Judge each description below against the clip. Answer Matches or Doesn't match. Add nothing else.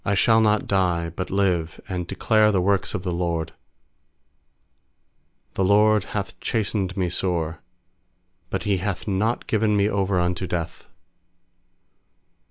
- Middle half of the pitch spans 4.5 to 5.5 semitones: Doesn't match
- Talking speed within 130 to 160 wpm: Matches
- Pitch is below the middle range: Matches